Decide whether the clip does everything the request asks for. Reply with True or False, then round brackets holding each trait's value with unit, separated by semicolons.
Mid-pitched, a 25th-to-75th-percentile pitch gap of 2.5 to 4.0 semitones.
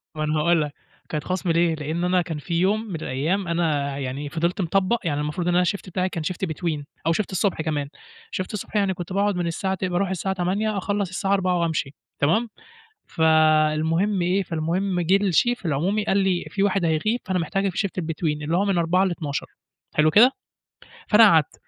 True (175 Hz; 3.5 semitones)